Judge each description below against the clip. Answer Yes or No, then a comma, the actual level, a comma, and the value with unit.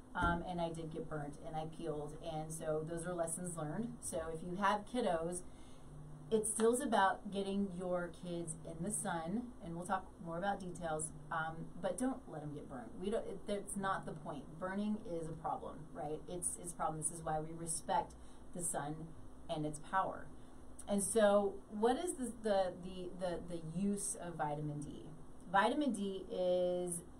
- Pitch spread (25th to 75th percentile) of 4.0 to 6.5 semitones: No, average, 3.6 semitones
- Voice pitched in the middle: Yes, medium, 175 Hz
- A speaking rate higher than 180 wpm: Yes, average, 190 wpm